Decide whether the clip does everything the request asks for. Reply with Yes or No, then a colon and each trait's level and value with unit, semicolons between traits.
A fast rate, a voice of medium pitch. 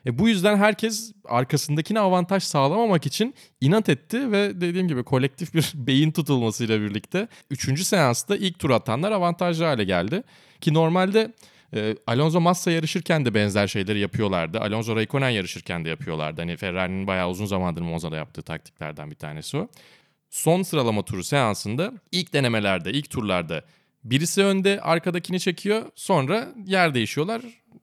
Yes: fast, 145 wpm; medium, 145 Hz